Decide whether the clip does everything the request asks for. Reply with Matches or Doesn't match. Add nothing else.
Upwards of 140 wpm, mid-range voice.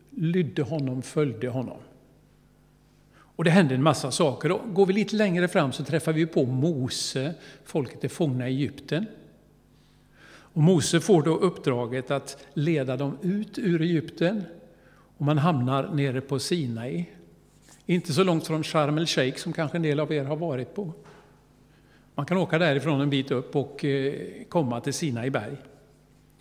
Matches